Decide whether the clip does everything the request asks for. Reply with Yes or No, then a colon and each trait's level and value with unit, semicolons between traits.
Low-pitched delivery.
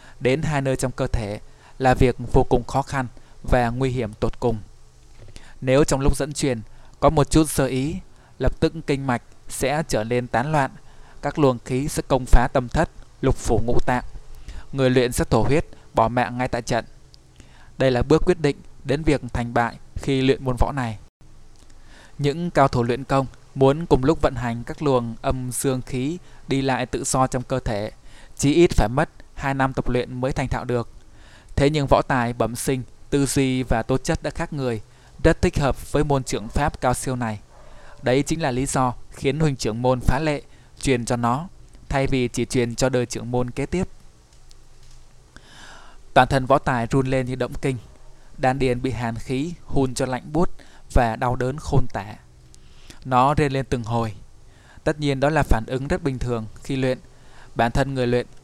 Yes: low, 130 Hz